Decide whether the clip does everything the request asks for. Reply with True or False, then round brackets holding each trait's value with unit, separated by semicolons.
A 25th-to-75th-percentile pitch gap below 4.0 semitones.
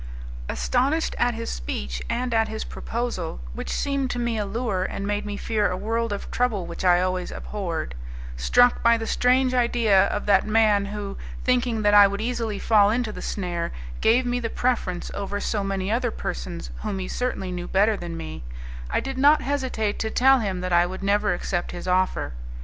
False (4.3 semitones)